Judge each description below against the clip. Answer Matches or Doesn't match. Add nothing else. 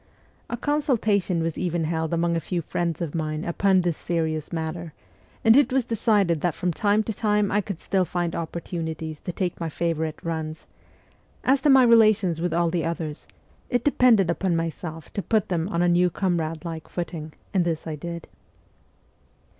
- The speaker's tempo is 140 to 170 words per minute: Doesn't match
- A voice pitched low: Doesn't match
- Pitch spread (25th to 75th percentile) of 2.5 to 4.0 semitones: Matches